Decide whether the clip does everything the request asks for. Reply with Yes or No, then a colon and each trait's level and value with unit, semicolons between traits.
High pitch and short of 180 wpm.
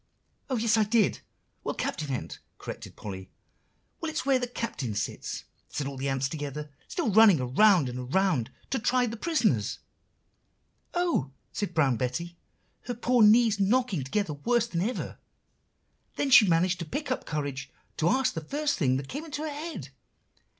Yes: high, 195 Hz; average, 170 wpm